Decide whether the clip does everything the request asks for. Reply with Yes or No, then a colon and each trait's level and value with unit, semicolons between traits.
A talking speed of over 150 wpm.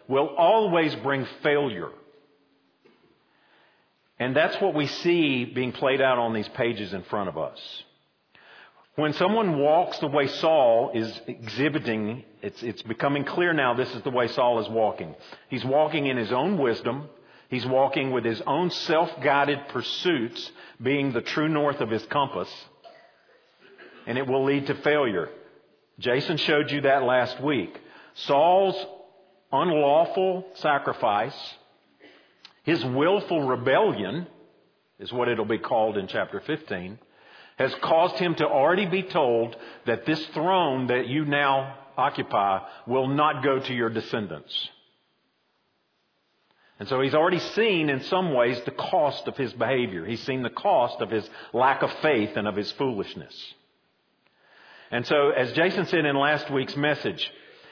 No: average, 145 wpm